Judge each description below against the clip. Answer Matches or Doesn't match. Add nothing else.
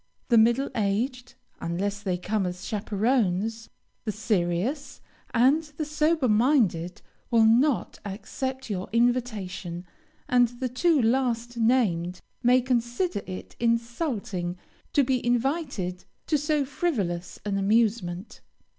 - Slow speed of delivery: Matches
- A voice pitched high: Matches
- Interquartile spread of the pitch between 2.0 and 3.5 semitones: Doesn't match